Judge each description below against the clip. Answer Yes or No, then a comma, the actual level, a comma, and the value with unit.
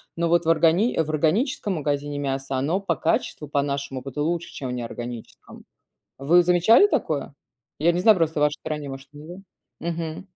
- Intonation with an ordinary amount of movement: Yes, average, 3.6 semitones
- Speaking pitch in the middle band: Yes, medium, 155 Hz